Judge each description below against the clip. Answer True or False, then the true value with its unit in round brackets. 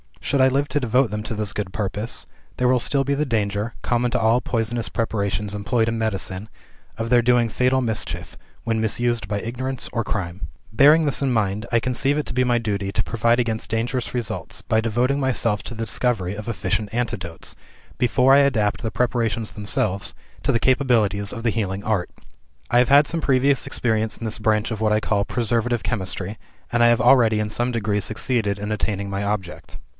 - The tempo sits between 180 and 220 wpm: True (200 wpm)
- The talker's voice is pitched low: True (115 Hz)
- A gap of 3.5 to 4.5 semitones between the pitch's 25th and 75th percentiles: False (2.9 semitones)